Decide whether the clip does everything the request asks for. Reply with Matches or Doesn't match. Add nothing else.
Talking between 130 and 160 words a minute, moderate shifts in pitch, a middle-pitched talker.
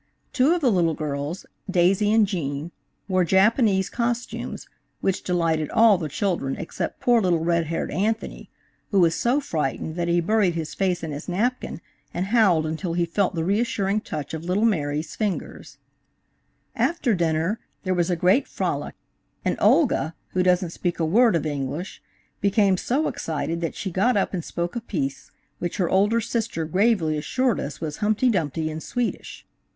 Doesn't match